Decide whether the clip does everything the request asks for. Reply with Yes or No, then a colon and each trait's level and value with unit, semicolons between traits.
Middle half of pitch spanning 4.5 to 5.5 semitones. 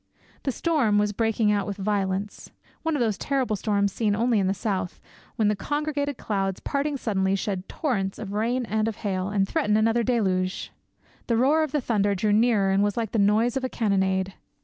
No: average, 3.5 semitones